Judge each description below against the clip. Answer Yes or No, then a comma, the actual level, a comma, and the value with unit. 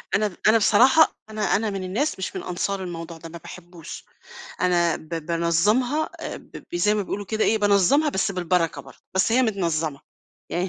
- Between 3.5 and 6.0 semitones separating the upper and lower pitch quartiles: Yes, average, 4.1 semitones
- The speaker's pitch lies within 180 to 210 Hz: Yes, high, 190 Hz